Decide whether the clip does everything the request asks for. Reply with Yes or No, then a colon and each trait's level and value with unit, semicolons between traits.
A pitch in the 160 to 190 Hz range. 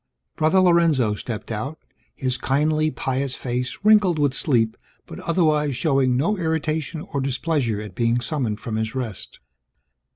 No: low, 135 Hz